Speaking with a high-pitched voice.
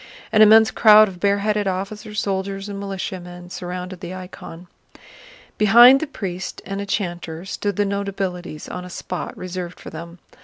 Yes: high, 195 Hz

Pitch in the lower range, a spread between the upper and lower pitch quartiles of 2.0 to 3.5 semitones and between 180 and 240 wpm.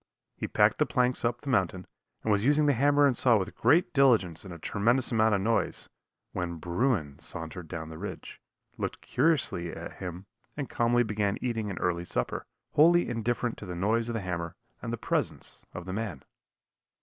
No: low, 105 Hz; wide, 5.5 semitones; average, 190 wpm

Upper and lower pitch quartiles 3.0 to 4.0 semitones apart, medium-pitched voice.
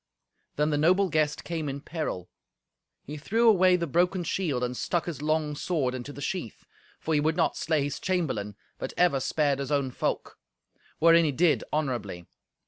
Yes: average, 3.7 semitones; medium, 155 Hz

